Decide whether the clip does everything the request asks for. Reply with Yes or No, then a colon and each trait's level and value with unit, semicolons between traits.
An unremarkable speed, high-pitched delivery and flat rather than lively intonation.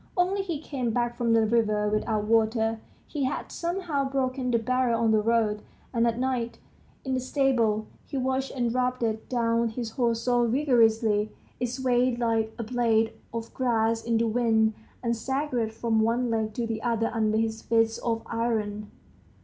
Yes: average, 175 wpm; high, 230 Hz; narrow, 2.1 semitones